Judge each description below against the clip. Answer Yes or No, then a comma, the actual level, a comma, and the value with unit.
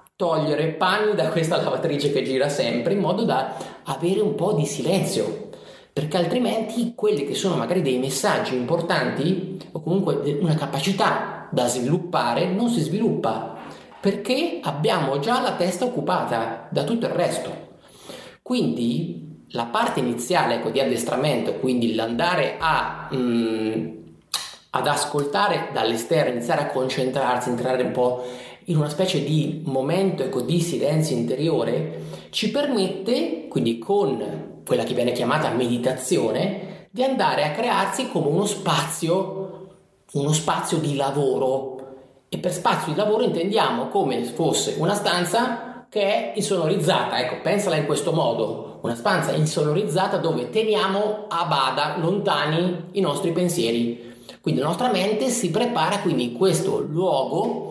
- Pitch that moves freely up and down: Yes, wide, 6.4 semitones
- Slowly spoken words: No, average, 135 wpm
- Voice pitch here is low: No, medium, 170 Hz